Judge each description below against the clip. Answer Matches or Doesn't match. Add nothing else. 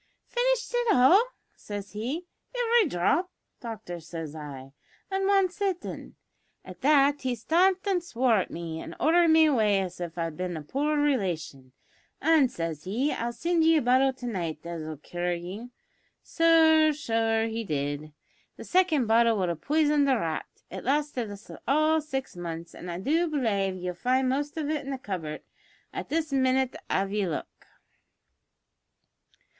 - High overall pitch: Matches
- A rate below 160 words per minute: Doesn't match